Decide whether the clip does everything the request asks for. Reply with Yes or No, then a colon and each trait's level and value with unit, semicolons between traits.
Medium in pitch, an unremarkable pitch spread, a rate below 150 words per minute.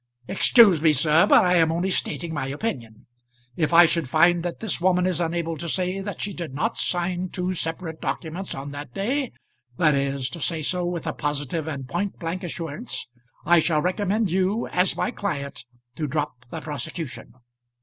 No: medium, 170 Hz; average, 3.4 semitones; average, 185 wpm